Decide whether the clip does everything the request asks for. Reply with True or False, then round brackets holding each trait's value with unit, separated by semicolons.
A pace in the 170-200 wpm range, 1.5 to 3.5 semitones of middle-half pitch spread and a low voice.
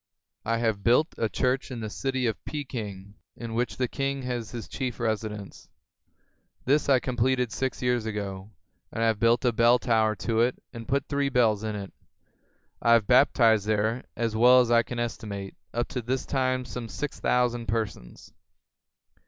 True (175 wpm; 2.6 semitones; 115 Hz)